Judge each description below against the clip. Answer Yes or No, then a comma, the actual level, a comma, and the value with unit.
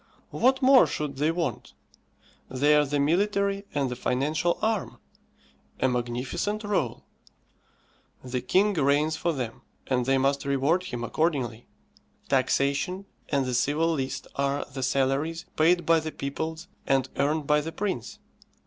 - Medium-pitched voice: Yes, medium, 145 Hz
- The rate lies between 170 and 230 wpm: No, average, 140 wpm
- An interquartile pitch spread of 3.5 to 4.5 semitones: Yes, average, 4.2 semitones